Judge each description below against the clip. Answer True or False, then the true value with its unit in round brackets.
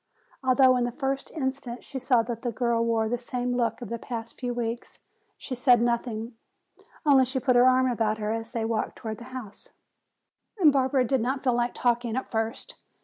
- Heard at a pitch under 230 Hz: False (245 Hz)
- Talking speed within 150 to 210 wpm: True (200 wpm)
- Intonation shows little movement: True (2.1 semitones)